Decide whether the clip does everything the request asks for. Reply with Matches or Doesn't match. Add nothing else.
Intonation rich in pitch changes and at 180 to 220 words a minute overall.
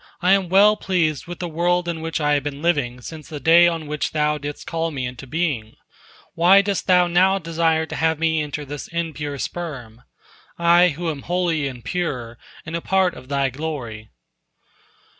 Doesn't match